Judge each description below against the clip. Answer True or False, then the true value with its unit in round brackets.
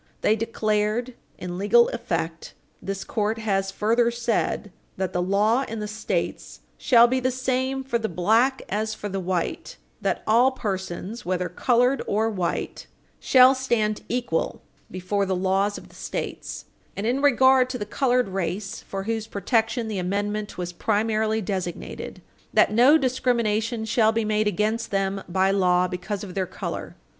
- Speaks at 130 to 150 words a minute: False (160 wpm)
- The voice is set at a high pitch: True (215 Hz)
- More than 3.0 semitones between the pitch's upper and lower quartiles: True (3.5 semitones)